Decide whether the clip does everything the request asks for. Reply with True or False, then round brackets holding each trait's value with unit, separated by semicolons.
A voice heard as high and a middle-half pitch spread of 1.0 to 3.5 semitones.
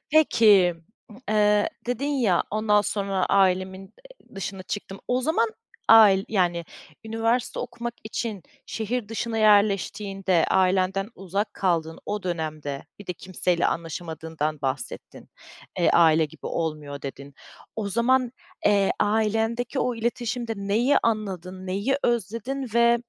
False (200 Hz; 4.1 semitones)